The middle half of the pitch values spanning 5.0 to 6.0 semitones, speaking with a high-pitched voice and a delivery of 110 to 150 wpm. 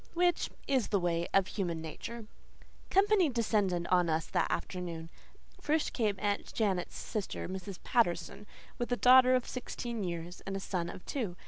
No: wide, 5.6 semitones; high, 200 Hz; average, 160 wpm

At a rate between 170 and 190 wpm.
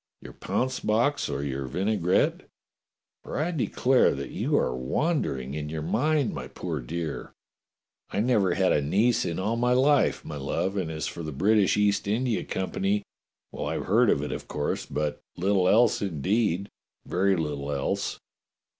Yes: average, 180 wpm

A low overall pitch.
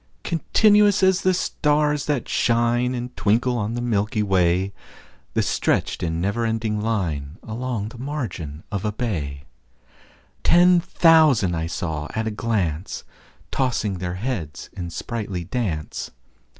Yes: low, 110 Hz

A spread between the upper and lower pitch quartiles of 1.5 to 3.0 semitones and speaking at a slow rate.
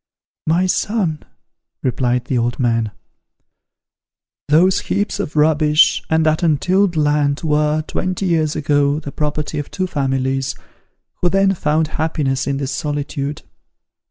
Yes: narrow, 2.5 semitones; slow, 130 wpm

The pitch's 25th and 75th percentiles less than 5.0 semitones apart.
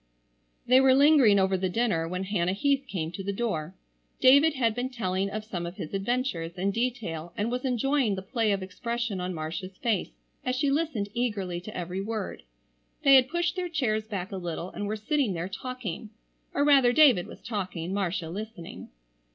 No: wide, 5.4 semitones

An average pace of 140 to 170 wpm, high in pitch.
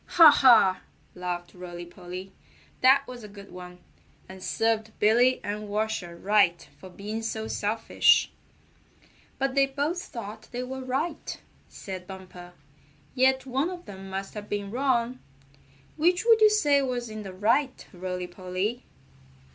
Yes: average, 145 wpm; high, 220 Hz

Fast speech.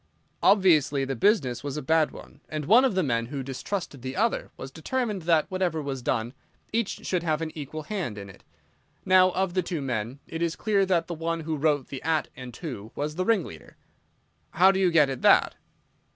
Yes: fast, 210 wpm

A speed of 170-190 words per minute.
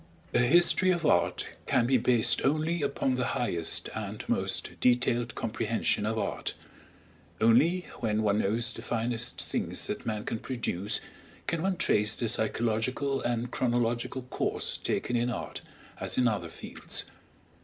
No: average, 145 wpm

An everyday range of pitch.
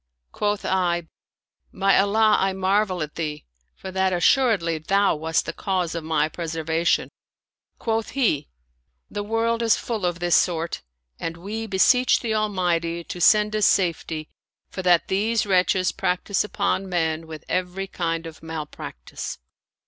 Yes: average, 3.8 semitones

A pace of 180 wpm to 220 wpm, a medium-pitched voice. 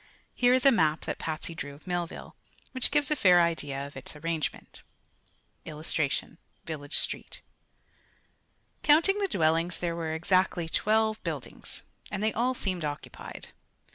No: average, 140 wpm; medium, 170 Hz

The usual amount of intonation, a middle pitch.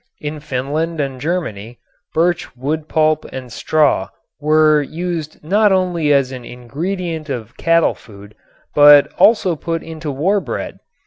Yes: average, 3.7 semitones; medium, 155 Hz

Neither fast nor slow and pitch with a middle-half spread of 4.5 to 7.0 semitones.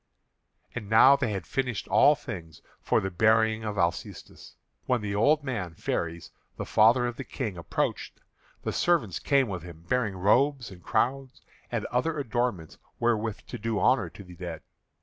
Yes: average, 170 wpm; wide, 5.4 semitones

